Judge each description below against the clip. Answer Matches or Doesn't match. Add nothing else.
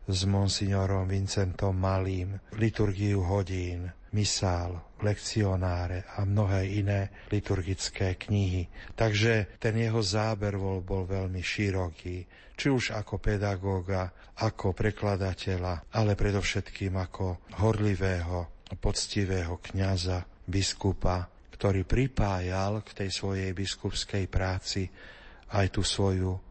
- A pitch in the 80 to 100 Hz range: Matches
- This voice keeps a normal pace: Doesn't match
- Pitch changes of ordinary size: Doesn't match